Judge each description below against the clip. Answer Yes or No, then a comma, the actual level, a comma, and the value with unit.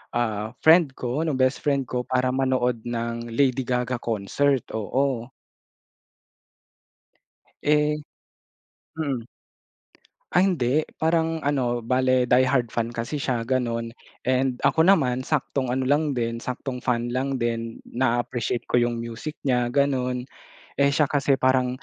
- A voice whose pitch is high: No, low, 130 Hz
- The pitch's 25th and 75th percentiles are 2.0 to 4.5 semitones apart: Yes, narrow, 2.6 semitones